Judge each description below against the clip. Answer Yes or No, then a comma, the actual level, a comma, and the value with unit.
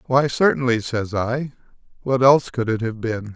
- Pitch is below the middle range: Yes, low, 125 Hz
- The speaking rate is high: No, average, 180 wpm